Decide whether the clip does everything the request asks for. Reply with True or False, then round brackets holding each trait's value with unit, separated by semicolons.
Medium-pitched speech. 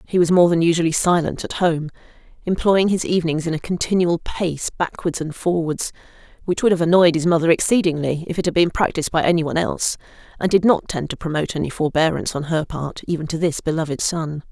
True (165 Hz)